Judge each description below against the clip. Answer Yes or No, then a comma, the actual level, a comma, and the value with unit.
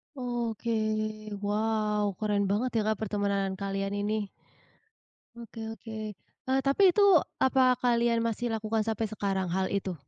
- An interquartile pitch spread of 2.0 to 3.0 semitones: Yes, average, 2.7 semitones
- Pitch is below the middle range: No, high, 220 Hz